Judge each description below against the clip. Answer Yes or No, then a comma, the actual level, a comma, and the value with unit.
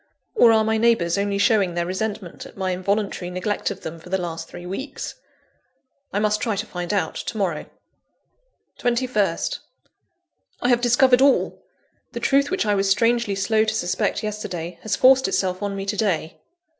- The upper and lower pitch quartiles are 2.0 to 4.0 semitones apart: Yes, average, 3.6 semitones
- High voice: Yes, high, 205 Hz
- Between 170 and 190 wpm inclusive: Yes, average, 175 wpm